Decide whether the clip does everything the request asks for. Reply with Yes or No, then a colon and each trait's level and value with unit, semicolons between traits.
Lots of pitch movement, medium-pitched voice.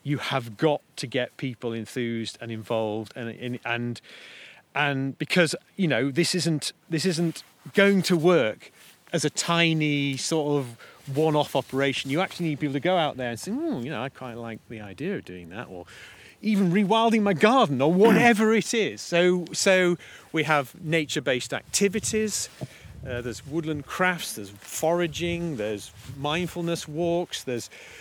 Yes: wide, 6.0 semitones; medium, 150 Hz